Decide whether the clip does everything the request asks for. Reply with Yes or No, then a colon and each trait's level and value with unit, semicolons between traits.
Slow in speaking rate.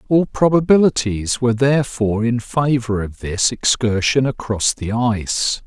Yes: slow, 125 wpm